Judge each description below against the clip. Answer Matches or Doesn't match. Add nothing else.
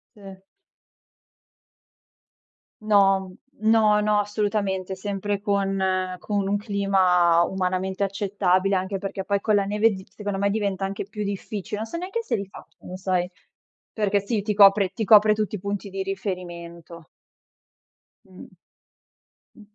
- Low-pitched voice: Doesn't match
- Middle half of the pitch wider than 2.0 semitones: Doesn't match